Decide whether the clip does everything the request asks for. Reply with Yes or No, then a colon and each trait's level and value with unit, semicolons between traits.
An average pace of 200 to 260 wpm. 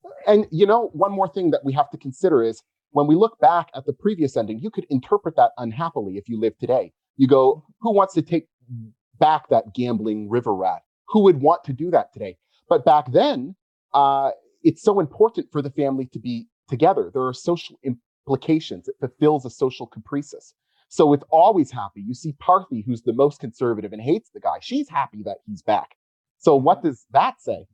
Yes: fast, 205 wpm